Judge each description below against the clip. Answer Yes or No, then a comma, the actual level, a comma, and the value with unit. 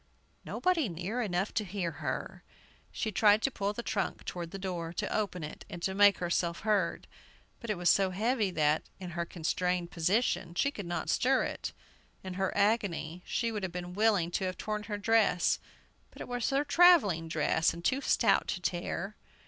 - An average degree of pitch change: Yes, average, 3.9 semitones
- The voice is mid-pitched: No, high, 195 Hz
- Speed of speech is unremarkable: Yes, average, 185 wpm